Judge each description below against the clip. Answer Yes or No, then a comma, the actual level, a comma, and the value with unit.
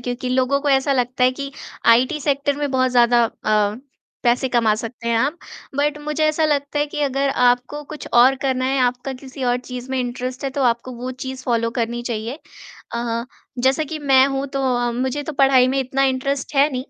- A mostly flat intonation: Yes, narrow, 2.2 semitones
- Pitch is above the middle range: Yes, very high, 260 Hz